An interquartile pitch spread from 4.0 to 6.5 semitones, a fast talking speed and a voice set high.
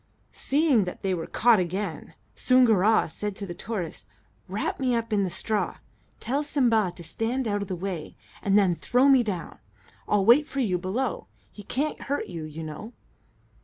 No: average, 5.1 semitones; average, 180 wpm; high, 210 Hz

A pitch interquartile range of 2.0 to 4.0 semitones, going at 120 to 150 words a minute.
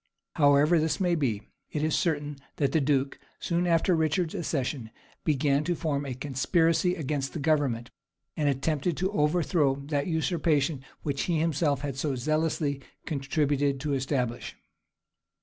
Yes: average, 2.8 semitones; average, 145 wpm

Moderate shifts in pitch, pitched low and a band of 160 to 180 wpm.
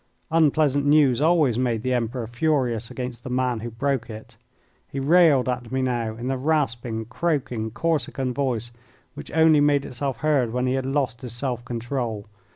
Yes: average, 3.2 semitones; low, 130 Hz; average, 170 wpm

